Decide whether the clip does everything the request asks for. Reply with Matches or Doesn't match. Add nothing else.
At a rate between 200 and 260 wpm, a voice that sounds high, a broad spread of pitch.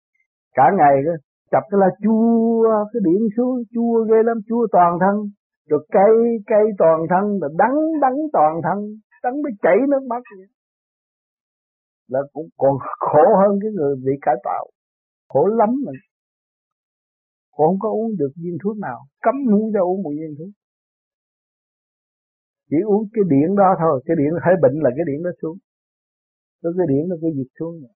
Doesn't match